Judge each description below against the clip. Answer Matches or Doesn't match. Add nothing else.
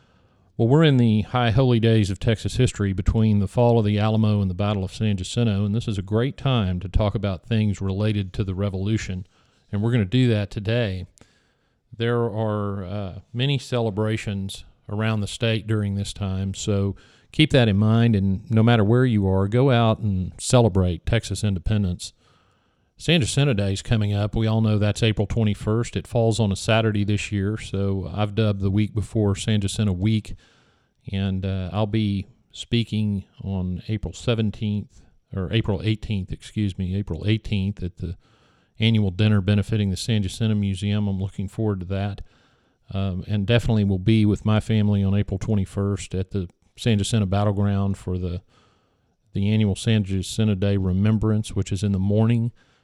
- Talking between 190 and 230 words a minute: Doesn't match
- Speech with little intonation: Matches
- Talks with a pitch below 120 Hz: Matches